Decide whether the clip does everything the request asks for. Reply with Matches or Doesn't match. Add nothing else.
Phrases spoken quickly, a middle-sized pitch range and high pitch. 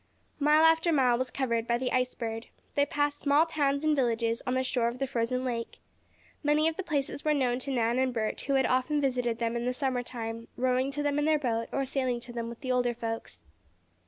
Matches